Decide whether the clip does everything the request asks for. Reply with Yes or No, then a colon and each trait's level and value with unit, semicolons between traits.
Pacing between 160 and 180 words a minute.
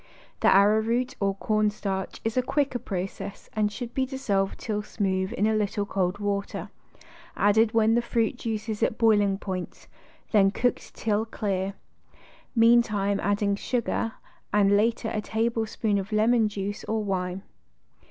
No: average, 150 wpm